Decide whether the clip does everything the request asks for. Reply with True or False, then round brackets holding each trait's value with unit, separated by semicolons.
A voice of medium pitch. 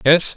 True (155 Hz)